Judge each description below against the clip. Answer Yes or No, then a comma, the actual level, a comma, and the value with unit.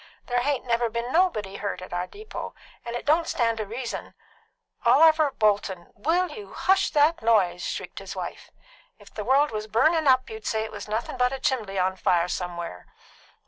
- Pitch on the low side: No, high, 235 Hz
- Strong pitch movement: Yes, wide, 6.2 semitones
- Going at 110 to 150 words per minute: No, average, 190 wpm